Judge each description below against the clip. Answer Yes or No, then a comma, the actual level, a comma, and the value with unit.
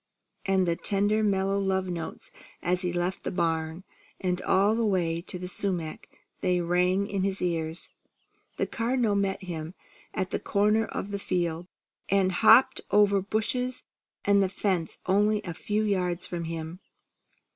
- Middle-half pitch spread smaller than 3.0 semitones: Yes, narrow, 2.5 semitones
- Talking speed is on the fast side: No, average, 155 wpm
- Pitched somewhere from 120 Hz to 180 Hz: No, high, 190 Hz